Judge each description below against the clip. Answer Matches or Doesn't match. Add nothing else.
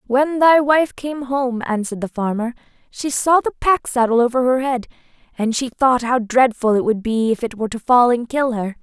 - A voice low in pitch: Doesn't match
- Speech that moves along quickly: Matches